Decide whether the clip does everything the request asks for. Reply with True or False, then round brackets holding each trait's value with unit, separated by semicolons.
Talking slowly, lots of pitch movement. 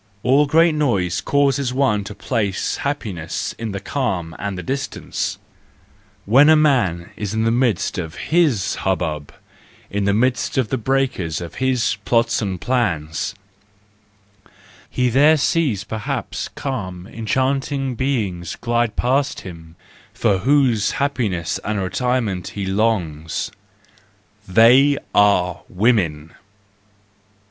True (120 wpm; 6.1 semitones)